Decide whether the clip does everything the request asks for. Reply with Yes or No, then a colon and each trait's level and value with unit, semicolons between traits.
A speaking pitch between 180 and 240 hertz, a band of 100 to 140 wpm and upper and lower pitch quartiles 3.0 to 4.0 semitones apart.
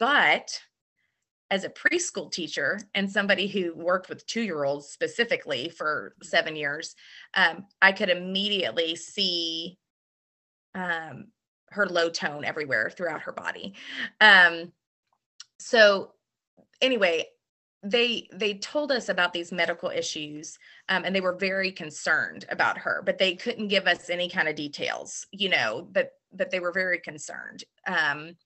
Yes: medium, 185 Hz; slow, 135 wpm; average, 3.7 semitones